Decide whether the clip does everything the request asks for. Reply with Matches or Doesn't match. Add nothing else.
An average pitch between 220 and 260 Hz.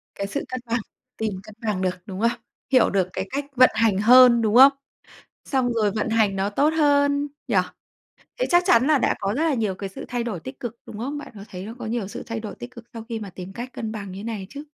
Matches